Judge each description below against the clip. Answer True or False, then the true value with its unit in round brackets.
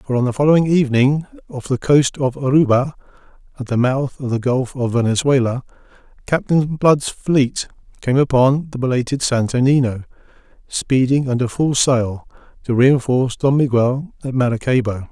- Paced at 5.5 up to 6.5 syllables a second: False (5.0 syllables/s)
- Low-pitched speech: True (130 Hz)